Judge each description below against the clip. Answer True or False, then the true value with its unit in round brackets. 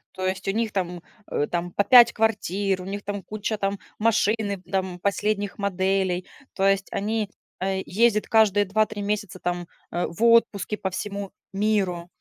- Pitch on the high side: True (200 Hz)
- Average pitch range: False (2.2 semitones)